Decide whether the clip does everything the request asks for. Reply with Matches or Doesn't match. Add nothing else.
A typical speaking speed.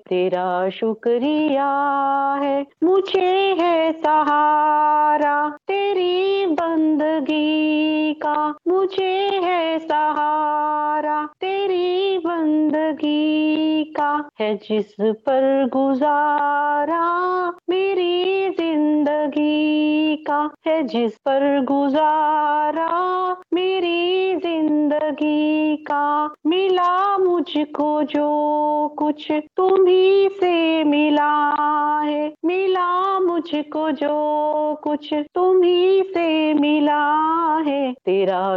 Doesn't match